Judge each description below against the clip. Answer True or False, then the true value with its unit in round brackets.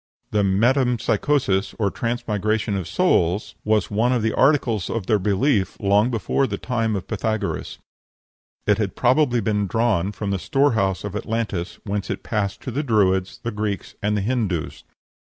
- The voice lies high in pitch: False (105 Hz)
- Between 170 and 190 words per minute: False (160 wpm)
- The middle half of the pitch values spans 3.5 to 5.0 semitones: False (3.1 semitones)